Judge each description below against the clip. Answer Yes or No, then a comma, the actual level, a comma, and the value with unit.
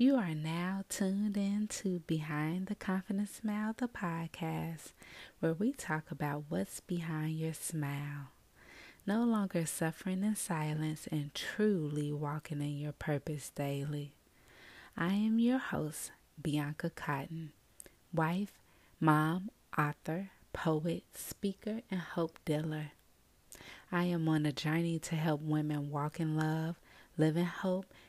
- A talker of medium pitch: Yes, medium, 160 Hz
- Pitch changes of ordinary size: Yes, average, 3.8 semitones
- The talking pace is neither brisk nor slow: No, slow, 130 wpm